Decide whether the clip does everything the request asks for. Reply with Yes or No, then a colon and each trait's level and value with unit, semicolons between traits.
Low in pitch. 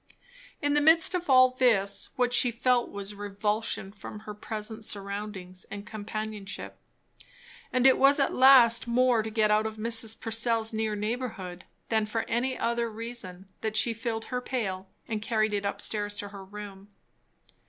No: high, 220 Hz